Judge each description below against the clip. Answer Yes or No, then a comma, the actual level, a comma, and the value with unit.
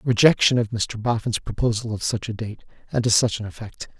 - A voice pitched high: No, low, 110 Hz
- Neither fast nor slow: No, fast, 210 wpm